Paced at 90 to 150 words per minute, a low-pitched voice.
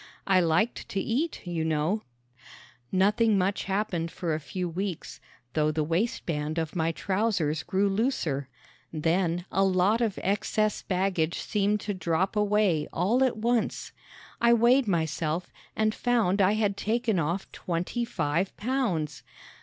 No: average, 140 wpm; high, 190 Hz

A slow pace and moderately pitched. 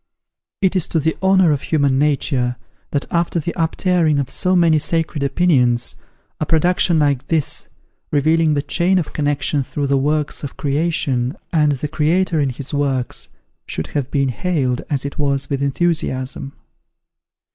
No: average, 155 wpm; medium, 150 Hz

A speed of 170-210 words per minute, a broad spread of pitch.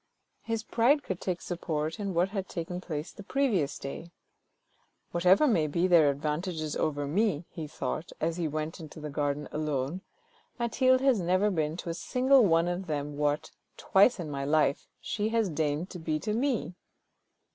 No: average, 180 wpm; average, 5.0 semitones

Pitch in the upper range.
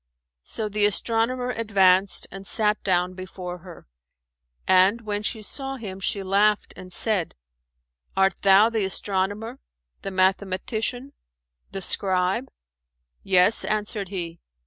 Yes: high, 195 Hz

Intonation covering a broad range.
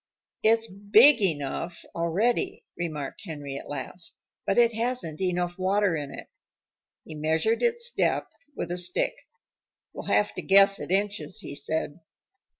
No: average, 4.8 semitones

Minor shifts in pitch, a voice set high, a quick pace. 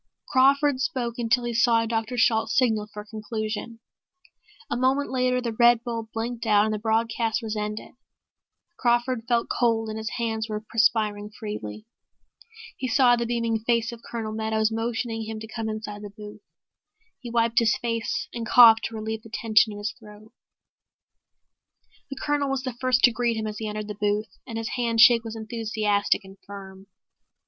No: narrow, 1.8 semitones; high, 225 Hz; average, 180 wpm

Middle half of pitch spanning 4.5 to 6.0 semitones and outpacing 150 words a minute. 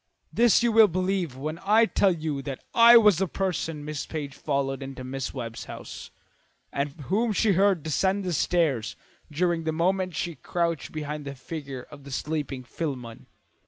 Yes: average, 5.2 semitones; average, 170 wpm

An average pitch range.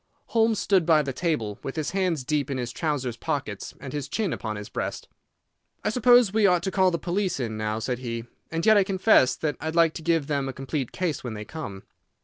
No: wide, 6.5 semitones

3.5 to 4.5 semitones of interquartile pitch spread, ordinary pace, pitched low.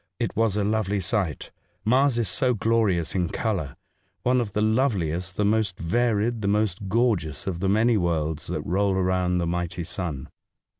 Yes: average, 4.1 semitones; average, 180 wpm; low, 100 Hz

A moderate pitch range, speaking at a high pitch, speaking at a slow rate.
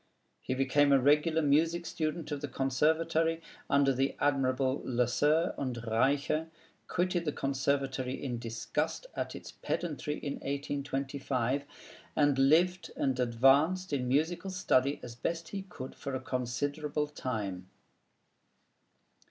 No: average, 3.2 semitones; medium, 140 Hz; slow, 125 wpm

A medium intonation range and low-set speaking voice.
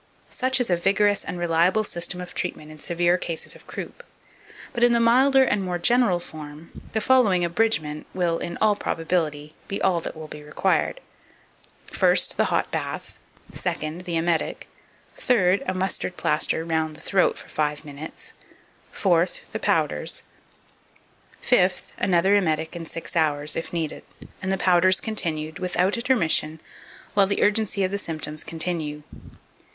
No: average, 3.8 semitones; medium, 175 Hz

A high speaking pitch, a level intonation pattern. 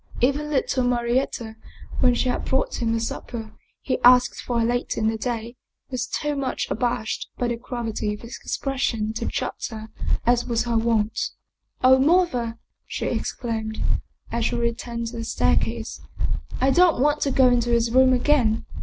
Yes: high, 240 Hz; narrow, 2.2 semitones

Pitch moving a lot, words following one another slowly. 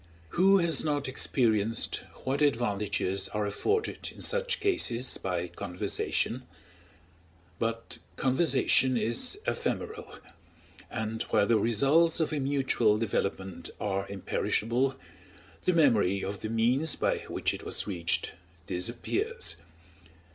Yes: wide, 6.0 semitones; slow, 110 wpm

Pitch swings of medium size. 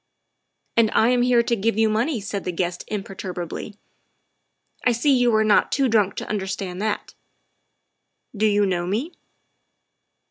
Yes: average, 3.3 semitones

